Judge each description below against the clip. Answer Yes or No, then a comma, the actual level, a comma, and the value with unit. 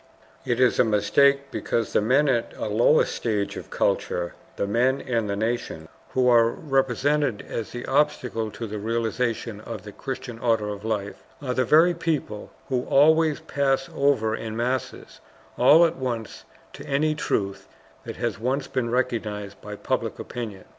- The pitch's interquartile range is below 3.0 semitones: No, average, 3.8 semitones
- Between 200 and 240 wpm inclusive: No, average, 165 wpm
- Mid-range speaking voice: No, low, 120 Hz